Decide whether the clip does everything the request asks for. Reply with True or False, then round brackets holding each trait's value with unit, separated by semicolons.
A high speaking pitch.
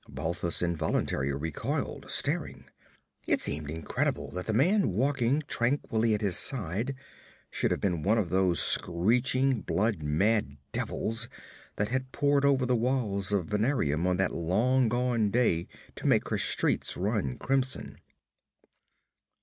False (105 Hz)